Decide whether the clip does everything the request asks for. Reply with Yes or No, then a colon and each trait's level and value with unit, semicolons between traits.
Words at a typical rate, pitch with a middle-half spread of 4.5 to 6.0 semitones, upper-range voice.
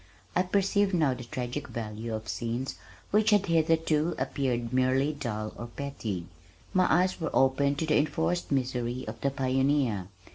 No: average, 155 wpm; average, 5.2 semitones; low, 135 Hz